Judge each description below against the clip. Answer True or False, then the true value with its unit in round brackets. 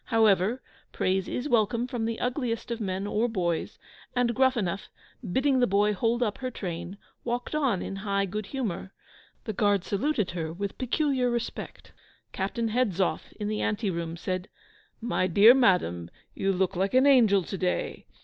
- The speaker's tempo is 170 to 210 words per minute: False (160 wpm)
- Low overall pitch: False (210 Hz)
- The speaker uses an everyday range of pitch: True (4.3 semitones)